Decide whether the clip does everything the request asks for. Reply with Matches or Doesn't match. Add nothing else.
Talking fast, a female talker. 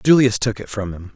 Doesn't match